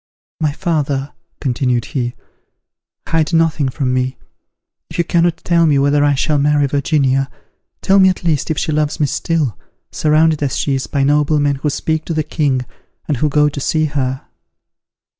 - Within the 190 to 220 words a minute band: No, average, 175 wpm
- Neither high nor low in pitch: Yes, medium, 145 Hz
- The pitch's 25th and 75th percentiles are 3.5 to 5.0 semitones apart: No, narrow, 2.4 semitones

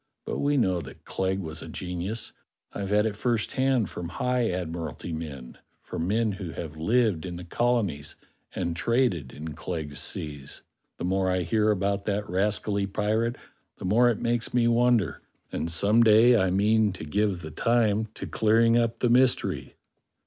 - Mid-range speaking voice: No, low, 100 Hz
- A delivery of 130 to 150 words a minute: No, average, 170 wpm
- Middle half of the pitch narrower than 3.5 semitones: No, average, 4.9 semitones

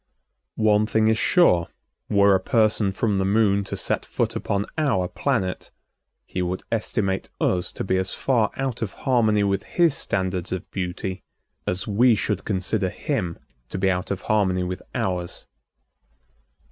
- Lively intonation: No, average, 2.8 semitones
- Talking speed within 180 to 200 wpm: No, average, 160 wpm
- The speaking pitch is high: No, low, 100 Hz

